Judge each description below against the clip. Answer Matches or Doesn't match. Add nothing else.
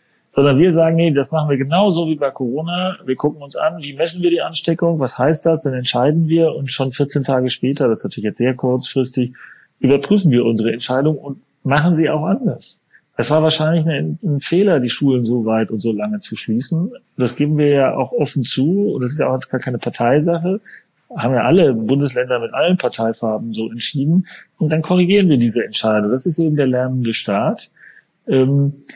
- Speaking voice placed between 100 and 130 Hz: Doesn't match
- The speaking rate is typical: Doesn't match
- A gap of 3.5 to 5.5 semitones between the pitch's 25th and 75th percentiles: Matches